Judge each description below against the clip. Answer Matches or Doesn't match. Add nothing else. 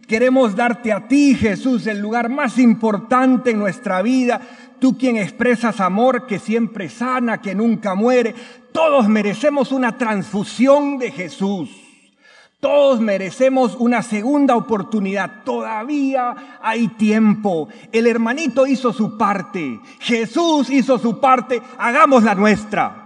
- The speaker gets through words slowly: Matches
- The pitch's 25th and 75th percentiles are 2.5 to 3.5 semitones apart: Matches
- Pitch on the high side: Matches